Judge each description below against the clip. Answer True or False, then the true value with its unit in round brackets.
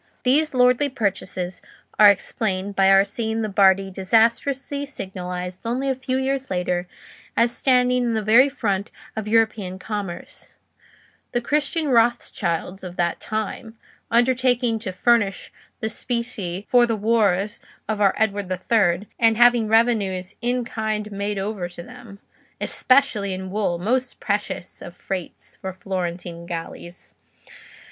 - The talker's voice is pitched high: True (215 Hz)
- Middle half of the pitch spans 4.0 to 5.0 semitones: True (4.3 semitones)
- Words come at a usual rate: False (130 wpm)